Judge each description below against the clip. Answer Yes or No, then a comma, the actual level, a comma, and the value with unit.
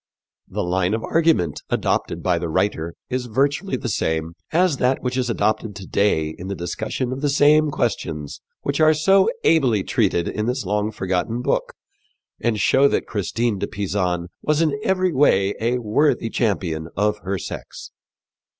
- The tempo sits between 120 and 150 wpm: No, average, 170 wpm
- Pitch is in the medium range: No, low, 110 Hz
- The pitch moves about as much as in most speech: No, wide, 7.0 semitones